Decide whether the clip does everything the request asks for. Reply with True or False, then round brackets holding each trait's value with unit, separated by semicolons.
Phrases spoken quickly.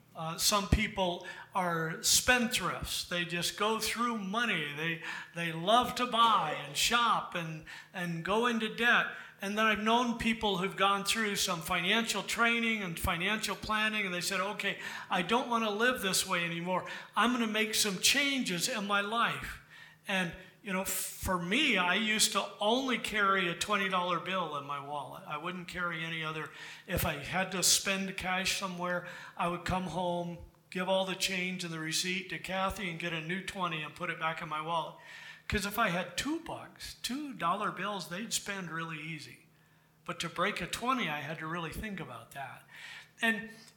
False (185 wpm)